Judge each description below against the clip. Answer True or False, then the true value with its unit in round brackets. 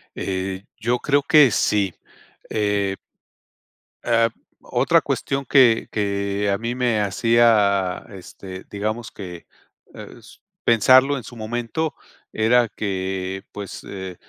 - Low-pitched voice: True (105 Hz)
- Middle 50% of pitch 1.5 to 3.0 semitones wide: False (3.5 semitones)